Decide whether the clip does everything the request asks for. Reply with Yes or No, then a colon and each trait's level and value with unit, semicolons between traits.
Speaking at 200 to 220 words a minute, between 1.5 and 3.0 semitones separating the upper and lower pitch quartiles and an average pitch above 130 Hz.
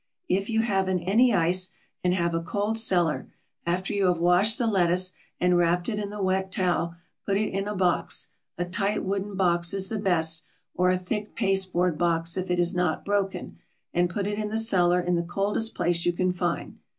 Yes: fast, 205 wpm; narrow, 2.4 semitones; medium, 185 Hz